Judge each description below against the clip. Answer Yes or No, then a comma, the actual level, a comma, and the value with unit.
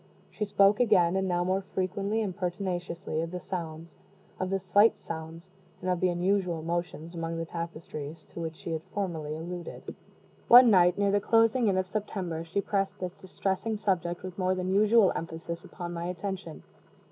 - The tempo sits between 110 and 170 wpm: No, average, 180 wpm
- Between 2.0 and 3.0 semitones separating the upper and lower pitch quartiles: Yes, average, 2.7 semitones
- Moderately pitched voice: Yes, medium, 180 Hz